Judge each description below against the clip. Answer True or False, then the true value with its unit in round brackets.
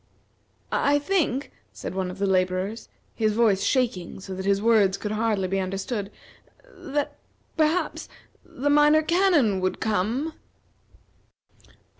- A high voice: True (220 Hz)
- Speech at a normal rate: False (125 wpm)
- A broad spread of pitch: True (7.0 semitones)